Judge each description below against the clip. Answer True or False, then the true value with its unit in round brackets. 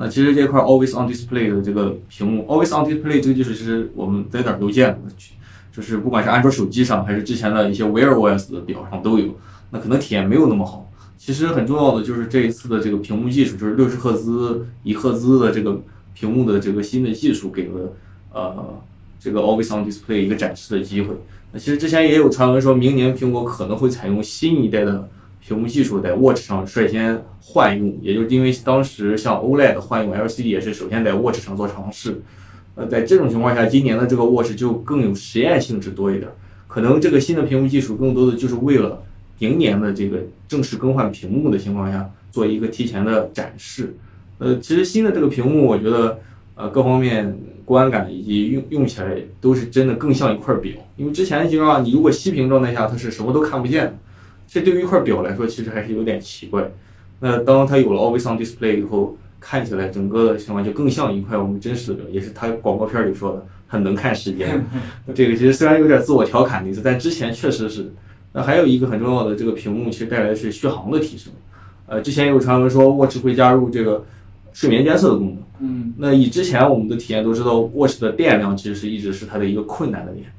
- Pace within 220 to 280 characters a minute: False (390 characters per minute)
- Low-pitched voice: True (110 Hz)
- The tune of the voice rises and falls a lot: False (4.1 semitones)